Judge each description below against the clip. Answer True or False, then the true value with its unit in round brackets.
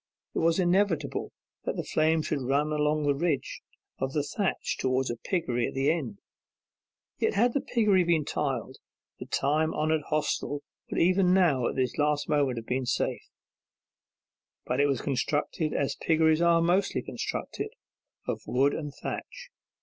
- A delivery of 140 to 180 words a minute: True (160 wpm)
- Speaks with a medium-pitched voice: True (150 Hz)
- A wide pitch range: False (3.8 semitones)